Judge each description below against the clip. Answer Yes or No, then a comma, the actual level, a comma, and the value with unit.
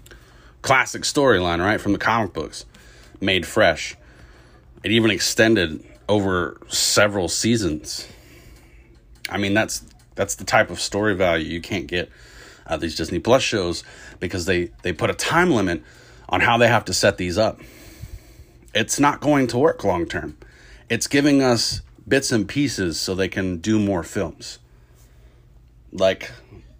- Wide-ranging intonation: Yes, wide, 5.8 semitones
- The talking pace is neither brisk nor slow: Yes, average, 150 wpm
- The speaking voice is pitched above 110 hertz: No, very low, 95 Hz